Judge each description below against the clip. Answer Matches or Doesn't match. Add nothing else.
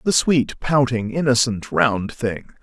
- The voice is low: Matches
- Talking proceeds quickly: Doesn't match